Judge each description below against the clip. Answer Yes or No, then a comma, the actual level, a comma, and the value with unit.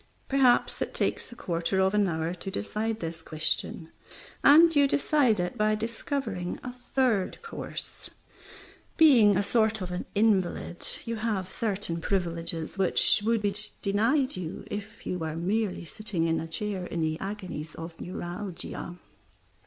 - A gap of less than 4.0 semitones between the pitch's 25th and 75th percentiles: No, average, 4.5 semitones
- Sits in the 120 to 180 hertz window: No, high, 200 Hz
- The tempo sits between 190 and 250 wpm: No, average, 150 wpm